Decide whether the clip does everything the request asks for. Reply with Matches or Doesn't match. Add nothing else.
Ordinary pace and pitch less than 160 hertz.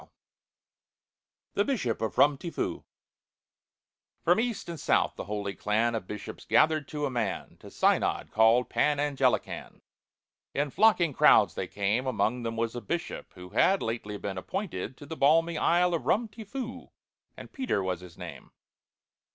Matches